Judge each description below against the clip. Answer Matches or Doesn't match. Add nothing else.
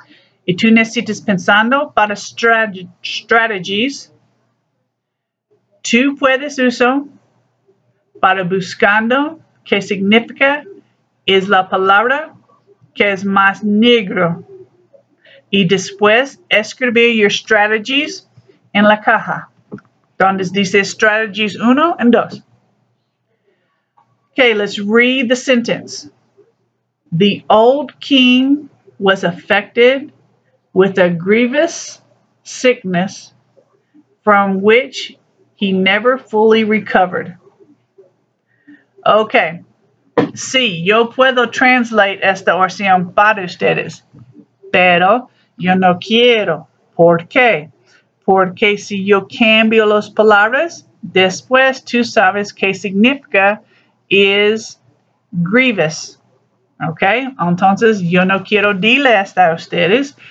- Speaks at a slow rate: Matches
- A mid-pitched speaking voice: Doesn't match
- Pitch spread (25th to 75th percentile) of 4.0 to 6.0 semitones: Matches